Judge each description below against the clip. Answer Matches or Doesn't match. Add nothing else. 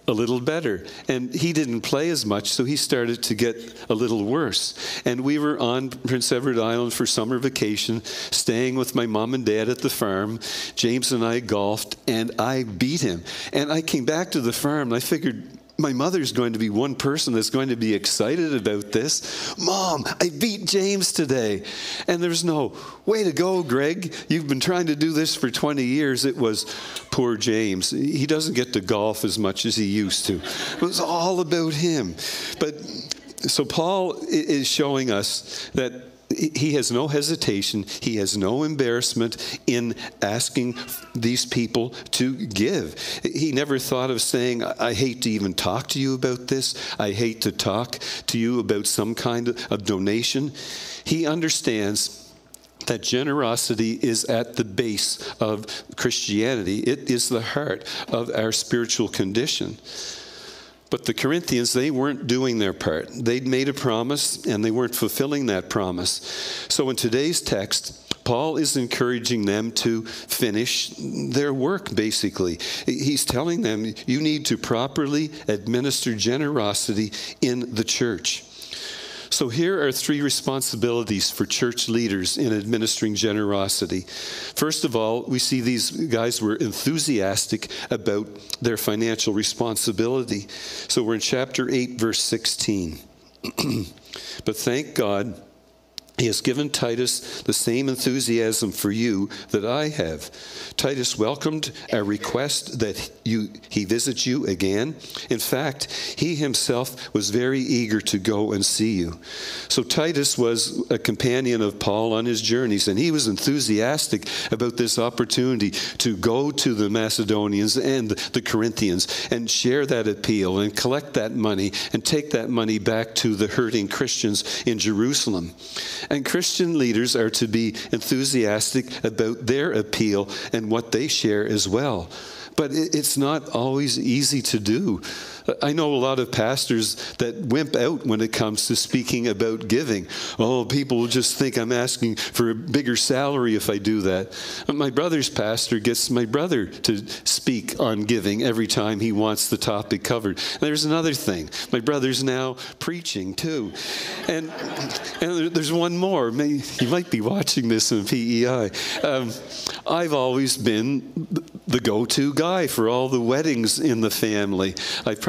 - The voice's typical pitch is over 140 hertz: Doesn't match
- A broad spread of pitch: Doesn't match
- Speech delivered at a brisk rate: Doesn't match